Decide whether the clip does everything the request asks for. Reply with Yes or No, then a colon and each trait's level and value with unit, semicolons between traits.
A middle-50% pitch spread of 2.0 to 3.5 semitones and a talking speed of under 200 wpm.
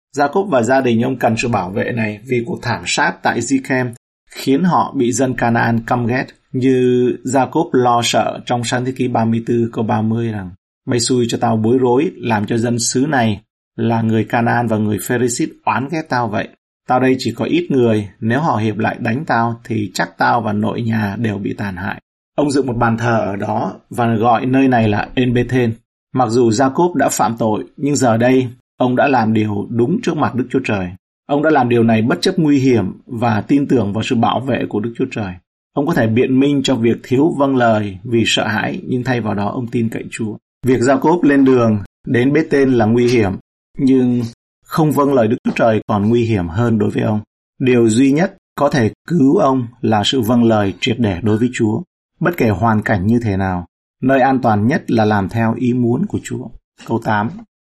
No: average, 2.7 semitones; average, 220 wpm